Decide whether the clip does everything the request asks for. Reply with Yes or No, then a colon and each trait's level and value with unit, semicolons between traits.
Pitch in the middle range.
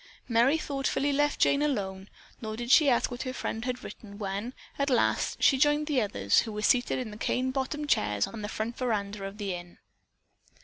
No: high, 240 Hz